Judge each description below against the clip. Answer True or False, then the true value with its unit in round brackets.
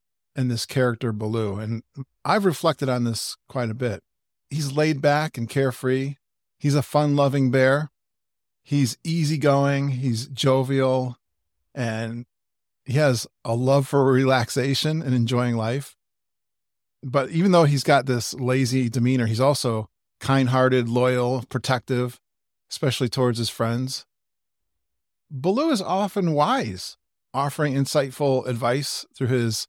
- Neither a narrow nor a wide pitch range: True (3.4 semitones)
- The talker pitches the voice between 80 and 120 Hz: False (130 Hz)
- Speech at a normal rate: False (125 wpm)